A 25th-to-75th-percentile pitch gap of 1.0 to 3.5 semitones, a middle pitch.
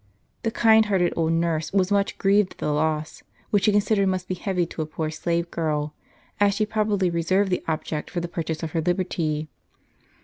No: average, 3.9 semitones; medium, 175 Hz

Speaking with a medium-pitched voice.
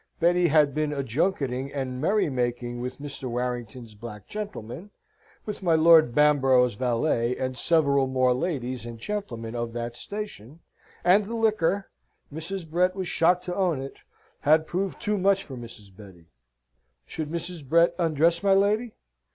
Yes: medium, 150 Hz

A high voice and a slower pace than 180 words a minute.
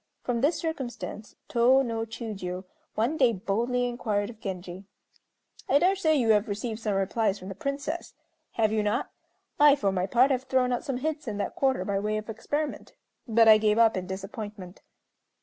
No: high, 225 Hz; average, 185 wpm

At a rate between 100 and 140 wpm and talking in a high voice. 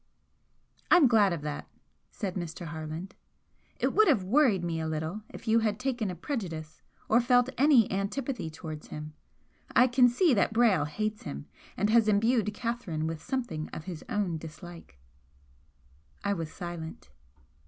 No: average, 155 wpm; high, 200 Hz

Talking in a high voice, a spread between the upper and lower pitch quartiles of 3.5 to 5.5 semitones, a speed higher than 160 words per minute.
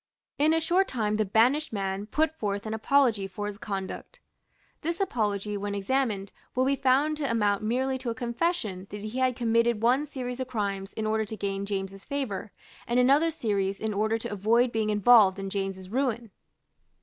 Yes: high, 220 Hz; average, 4.3 semitones; average, 185 wpm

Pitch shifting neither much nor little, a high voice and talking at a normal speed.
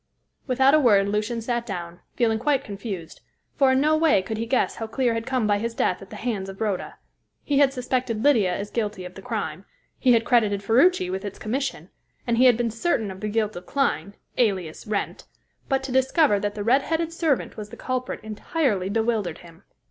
No: average, 4.4 semitones; high, 225 Hz; fast, 210 wpm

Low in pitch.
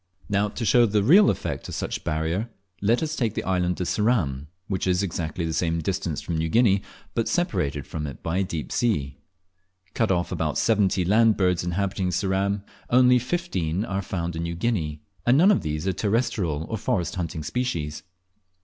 Yes: very low, 95 Hz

